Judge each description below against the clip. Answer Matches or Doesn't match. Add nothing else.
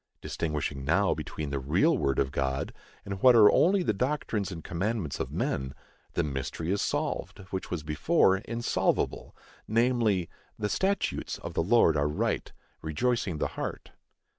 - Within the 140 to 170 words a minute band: Matches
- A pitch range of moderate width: Doesn't match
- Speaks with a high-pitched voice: Doesn't match